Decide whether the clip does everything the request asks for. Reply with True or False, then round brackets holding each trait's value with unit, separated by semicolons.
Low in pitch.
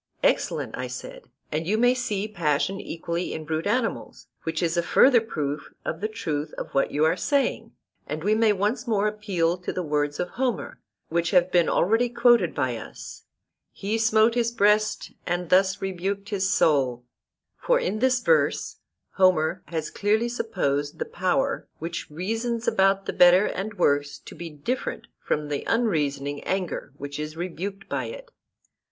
False (190 Hz)